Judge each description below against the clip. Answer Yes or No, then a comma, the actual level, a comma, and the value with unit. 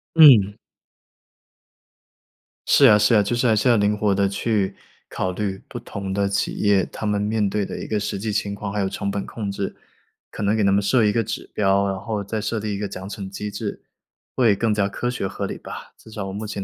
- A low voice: Yes, low, 105 Hz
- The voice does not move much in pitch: Yes, narrow, 1.5 semitones